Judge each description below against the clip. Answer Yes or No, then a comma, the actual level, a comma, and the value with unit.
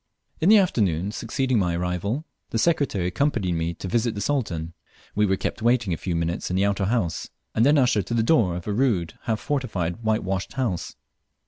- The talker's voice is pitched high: No, low, 105 Hz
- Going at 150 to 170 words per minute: No, fast, 205 wpm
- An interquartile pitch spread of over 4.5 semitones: Yes, wide, 5.6 semitones